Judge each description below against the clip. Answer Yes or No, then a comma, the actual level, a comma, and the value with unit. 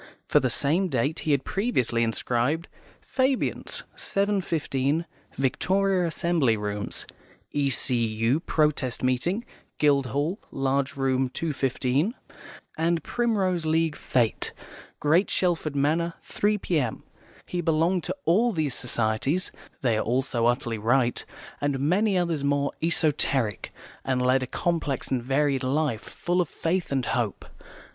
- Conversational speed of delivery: No, slow, 125 wpm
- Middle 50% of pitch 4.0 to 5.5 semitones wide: Yes, average, 5.0 semitones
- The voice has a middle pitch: Yes, medium, 145 Hz